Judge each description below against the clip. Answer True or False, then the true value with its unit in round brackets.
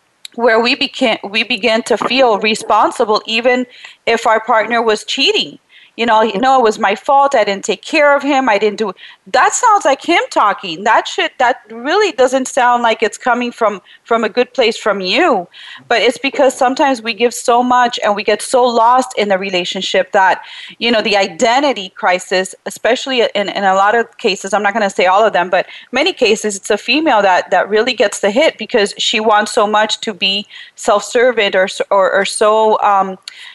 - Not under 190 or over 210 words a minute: True (200 wpm)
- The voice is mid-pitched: False (225 Hz)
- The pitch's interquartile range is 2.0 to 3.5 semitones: False (3.9 semitones)